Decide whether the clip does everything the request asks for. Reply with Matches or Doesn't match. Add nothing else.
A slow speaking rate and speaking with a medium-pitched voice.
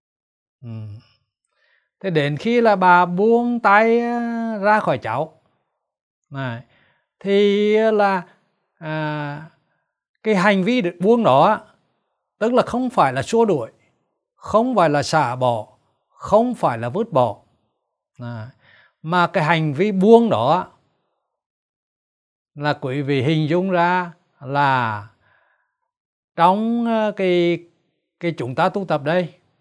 Matches